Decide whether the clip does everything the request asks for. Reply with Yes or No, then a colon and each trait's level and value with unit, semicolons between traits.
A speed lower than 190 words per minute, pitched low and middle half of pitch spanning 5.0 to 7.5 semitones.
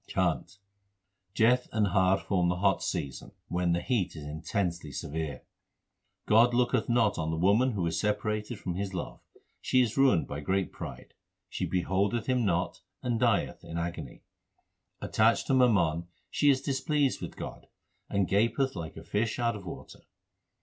Yes: average, 165 wpm; low, 100 Hz; wide, 5.4 semitones